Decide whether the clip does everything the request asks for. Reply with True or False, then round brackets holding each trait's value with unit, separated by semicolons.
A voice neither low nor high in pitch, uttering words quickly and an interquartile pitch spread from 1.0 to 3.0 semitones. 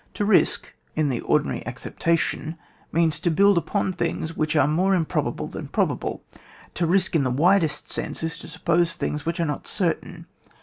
False (165 Hz; 180 wpm; 2.4 semitones)